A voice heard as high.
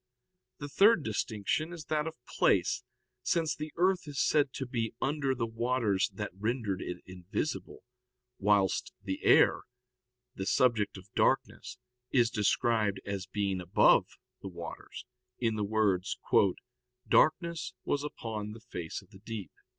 No: low, 110 Hz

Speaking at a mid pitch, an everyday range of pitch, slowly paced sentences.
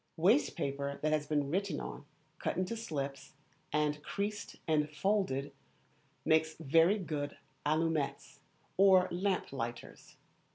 Yes: medium, 155 Hz; average, 4.5 semitones; slow, 120 wpm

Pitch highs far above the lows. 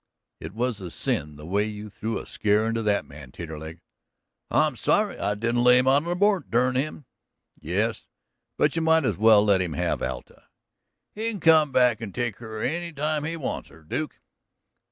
Yes: wide, 6.7 semitones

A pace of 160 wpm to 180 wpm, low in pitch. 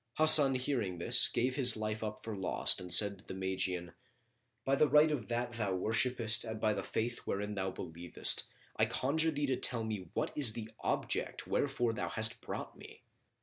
No: average, 190 wpm; low, 110 Hz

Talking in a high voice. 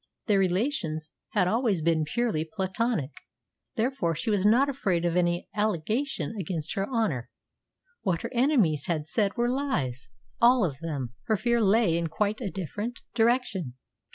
Yes: high, 195 Hz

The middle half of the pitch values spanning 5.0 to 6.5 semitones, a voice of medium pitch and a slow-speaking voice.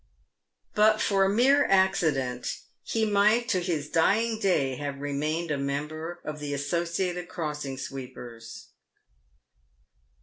Yes: wide, 5.5 semitones; medium, 165 Hz; slow, 115 wpm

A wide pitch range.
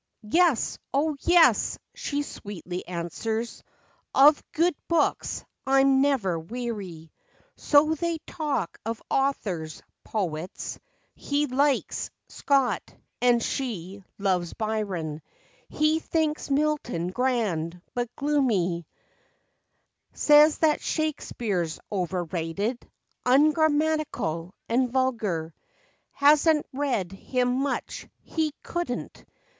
Yes: wide, 8.1 semitones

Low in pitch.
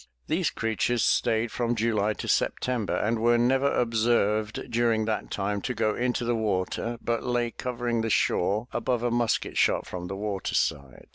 Yes: low, 115 Hz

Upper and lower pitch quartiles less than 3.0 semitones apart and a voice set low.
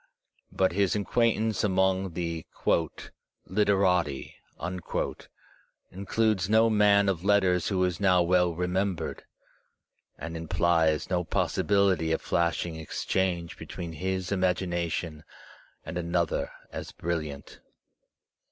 Yes: narrow, 2.6 semitones; very low, 90 Hz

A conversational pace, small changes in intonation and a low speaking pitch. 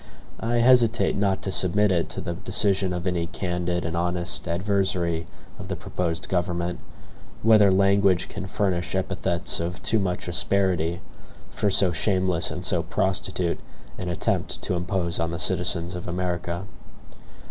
Yes: average, 145 wpm; narrow, 2.0 semitones; very low, 90 Hz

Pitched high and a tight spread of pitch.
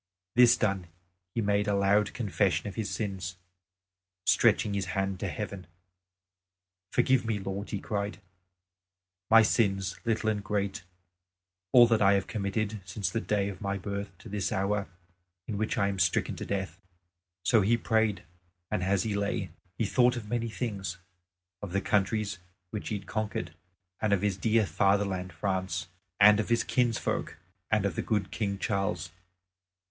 No: low, 100 Hz; narrow, 1.9 semitones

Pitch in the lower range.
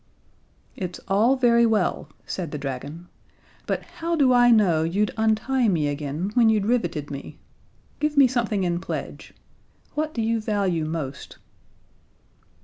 No: high, 205 Hz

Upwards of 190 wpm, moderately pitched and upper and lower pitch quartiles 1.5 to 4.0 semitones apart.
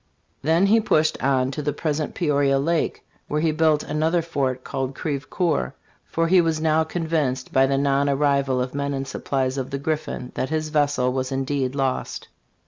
No: average, 180 wpm; medium, 145 Hz; average, 2.8 semitones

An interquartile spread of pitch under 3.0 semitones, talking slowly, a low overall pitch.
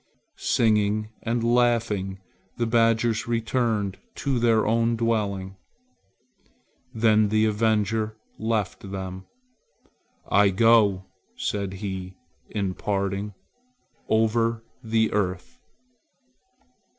Yes: narrow, 2.5 semitones; slow, 85 wpm; low, 110 Hz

